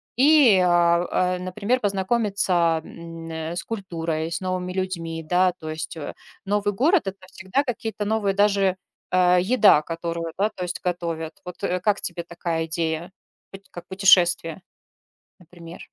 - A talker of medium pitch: Yes, medium, 180 Hz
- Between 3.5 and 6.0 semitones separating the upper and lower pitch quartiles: No, average, 3.0 semitones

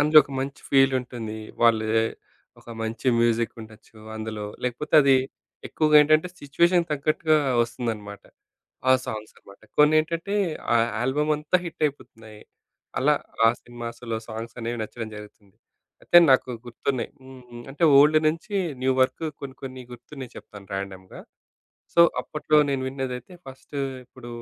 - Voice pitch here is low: Yes, low, 130 Hz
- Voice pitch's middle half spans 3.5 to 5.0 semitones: Yes, average, 4.7 semitones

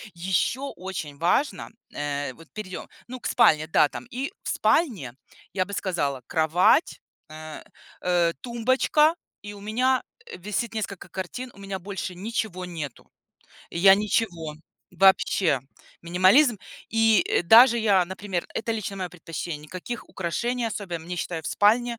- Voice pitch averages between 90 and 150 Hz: No, high, 190 Hz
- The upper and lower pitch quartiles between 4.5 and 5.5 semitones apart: Yes, average, 4.9 semitones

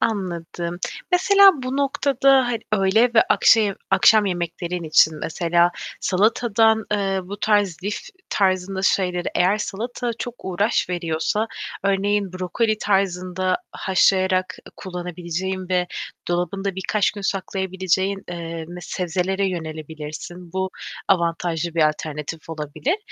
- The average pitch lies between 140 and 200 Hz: Yes, medium, 185 Hz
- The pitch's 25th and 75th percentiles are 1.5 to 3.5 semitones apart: Yes, average, 2.9 semitones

